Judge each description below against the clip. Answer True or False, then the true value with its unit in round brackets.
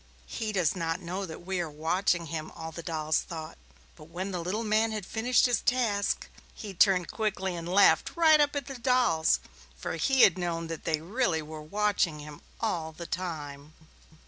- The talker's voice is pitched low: False (180 Hz)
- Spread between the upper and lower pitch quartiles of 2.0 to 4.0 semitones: False (4.9 semitones)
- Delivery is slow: False (185 wpm)